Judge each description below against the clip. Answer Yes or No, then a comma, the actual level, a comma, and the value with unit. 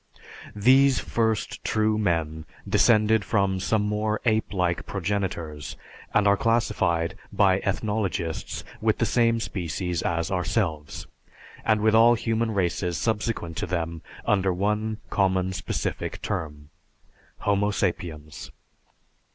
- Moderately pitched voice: No, low, 100 Hz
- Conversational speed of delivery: No, slow, 115 wpm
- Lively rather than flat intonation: No, average, 4.1 semitones